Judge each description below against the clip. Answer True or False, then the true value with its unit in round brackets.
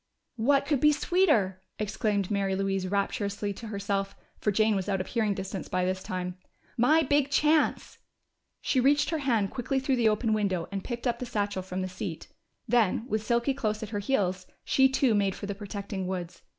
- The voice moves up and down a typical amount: True (4.3 semitones)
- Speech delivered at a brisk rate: False (195 wpm)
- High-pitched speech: True (210 Hz)